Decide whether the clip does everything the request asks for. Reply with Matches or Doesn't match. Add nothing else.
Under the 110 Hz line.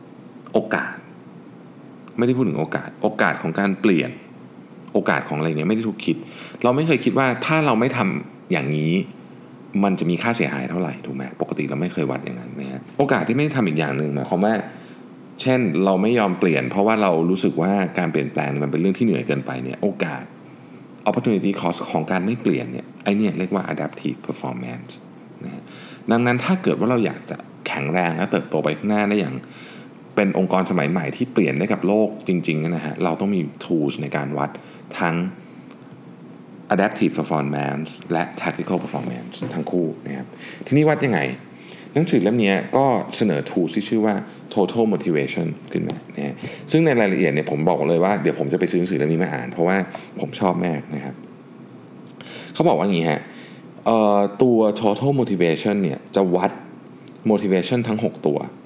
Matches